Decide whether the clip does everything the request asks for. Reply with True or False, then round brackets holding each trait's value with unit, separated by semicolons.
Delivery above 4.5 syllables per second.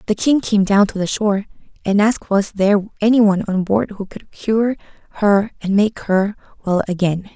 True (5.2 syllables/s)